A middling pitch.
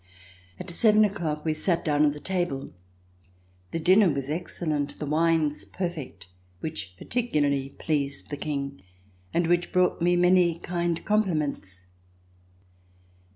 Yes: medium, 160 Hz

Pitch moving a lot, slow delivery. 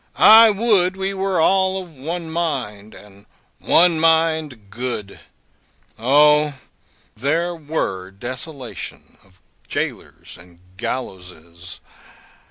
Yes: wide, 8.6 semitones; slow, 95 wpm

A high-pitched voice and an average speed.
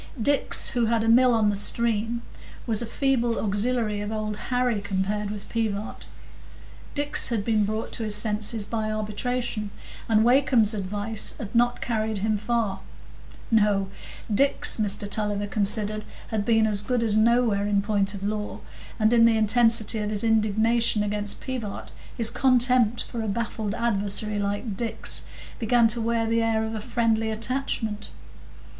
Yes: high, 220 Hz; average, 160 wpm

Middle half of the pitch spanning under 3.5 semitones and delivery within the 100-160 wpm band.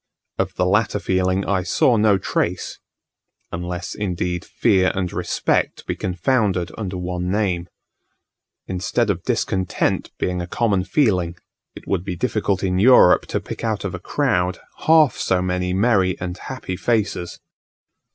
Yes: narrow, 2.5 semitones; average, 145 wpm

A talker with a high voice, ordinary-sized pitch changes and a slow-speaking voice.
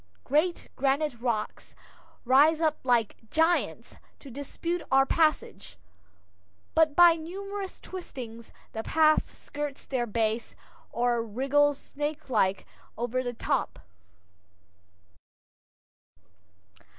Yes: very high, 275 Hz; average, 4.8 semitones; slow, 90 wpm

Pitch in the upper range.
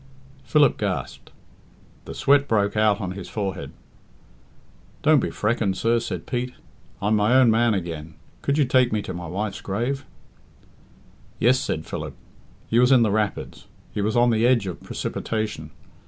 No: low, 110 Hz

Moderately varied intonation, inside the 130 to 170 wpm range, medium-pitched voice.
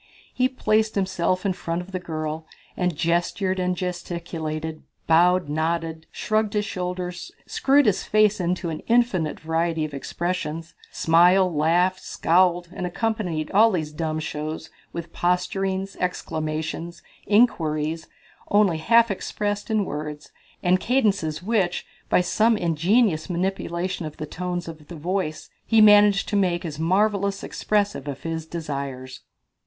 Yes: average, 3.5 semitones; slow, 135 wpm; medium, 175 Hz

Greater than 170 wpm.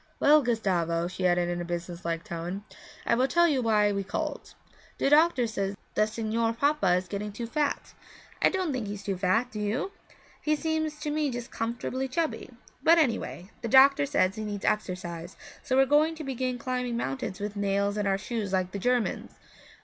Yes: average, 195 wpm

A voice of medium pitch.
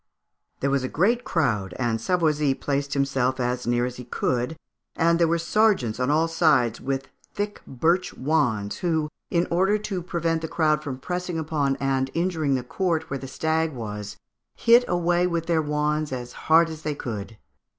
Yes: medium, 150 Hz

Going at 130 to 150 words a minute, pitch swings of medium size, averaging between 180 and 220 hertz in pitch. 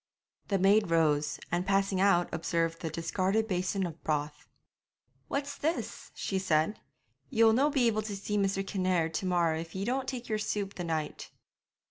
No: average, 170 wpm; average, 4.2 semitones; high, 190 Hz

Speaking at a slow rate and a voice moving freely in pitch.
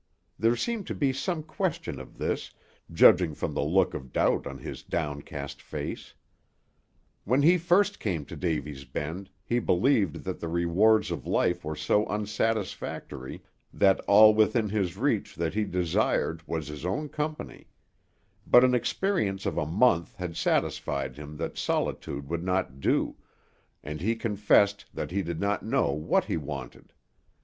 No: average, 155 wpm; wide, 6.4 semitones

